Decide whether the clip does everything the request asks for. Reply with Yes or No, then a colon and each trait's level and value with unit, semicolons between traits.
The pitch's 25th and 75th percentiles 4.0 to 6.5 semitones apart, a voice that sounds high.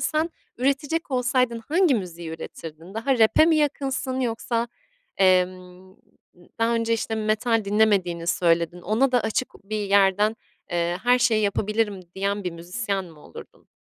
Yes: average, 5.0 semitones; high, 215 Hz